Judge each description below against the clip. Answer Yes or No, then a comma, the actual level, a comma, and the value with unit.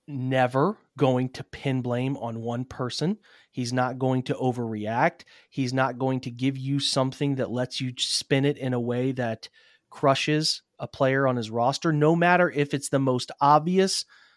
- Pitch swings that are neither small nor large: No, narrow, 2.2 semitones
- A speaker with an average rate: Yes, average, 175 wpm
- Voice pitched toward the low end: Yes, low, 130 Hz